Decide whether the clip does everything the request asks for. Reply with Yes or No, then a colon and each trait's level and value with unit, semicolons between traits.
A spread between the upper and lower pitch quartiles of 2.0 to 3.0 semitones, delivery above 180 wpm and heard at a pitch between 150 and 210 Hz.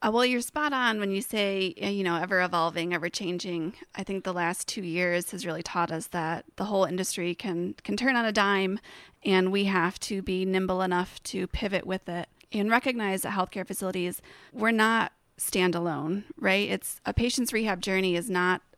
Yes: narrow, 2.5 semitones; average, 190 wpm; high, 190 Hz